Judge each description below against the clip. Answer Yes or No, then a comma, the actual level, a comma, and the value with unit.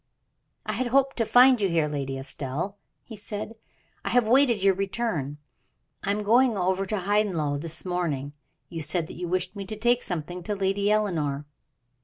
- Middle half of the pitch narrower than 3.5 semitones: No, average, 4.8 semitones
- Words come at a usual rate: Yes, average, 185 wpm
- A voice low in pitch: No, high, 195 Hz